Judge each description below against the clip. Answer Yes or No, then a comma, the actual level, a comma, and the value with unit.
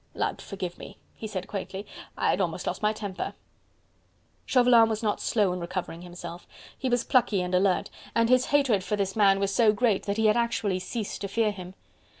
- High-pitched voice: Yes, high, 205 Hz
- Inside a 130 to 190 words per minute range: No, average, 200 wpm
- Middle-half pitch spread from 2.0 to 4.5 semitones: Yes, average, 3.3 semitones